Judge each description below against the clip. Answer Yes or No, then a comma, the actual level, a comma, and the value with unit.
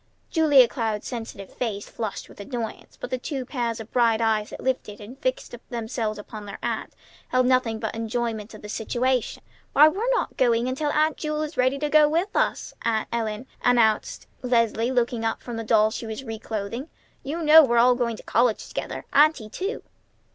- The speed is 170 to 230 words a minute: Yes, average, 190 wpm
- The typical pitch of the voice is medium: No, high, 240 Hz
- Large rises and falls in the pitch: No, average, 3.2 semitones